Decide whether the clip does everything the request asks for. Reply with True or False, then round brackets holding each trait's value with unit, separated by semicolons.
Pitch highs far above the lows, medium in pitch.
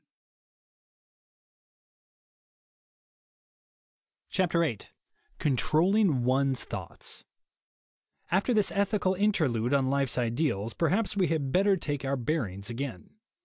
True (7.2 semitones; 145 Hz)